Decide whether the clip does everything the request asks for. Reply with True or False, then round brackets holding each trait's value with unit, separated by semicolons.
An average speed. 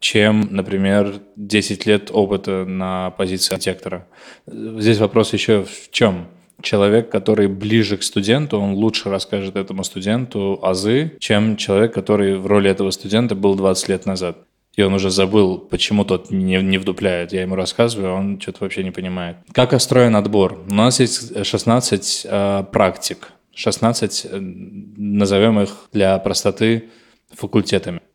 True (145 wpm)